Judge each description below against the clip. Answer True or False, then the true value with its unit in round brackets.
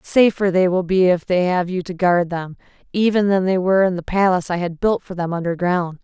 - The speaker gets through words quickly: True (240 wpm)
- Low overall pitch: False (180 Hz)